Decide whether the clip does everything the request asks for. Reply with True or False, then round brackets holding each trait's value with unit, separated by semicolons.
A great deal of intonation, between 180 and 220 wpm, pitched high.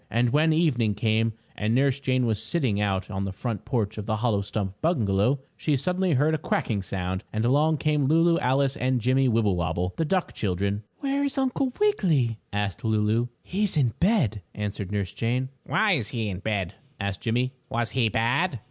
False (6.2 semitones; 190 wpm; 120 Hz)